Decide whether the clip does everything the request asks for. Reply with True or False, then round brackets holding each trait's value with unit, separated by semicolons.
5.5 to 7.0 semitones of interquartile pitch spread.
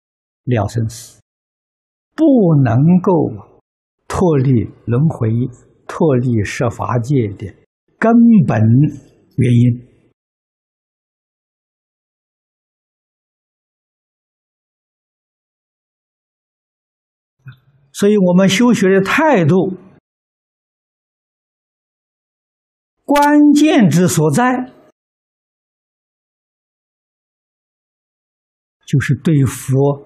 False (7.4 semitones)